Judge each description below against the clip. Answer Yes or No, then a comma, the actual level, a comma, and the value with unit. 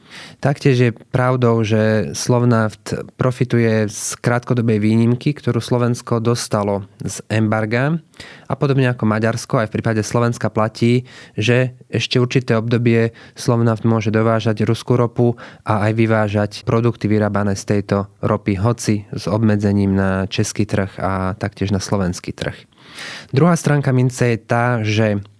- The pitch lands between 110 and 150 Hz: Yes, low, 115 Hz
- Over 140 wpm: No, average, 135 wpm